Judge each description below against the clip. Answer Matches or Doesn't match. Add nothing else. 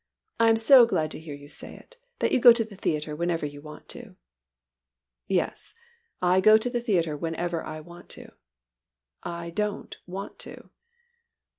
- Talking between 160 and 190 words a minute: Matches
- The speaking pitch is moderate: Matches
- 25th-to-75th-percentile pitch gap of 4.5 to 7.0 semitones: Matches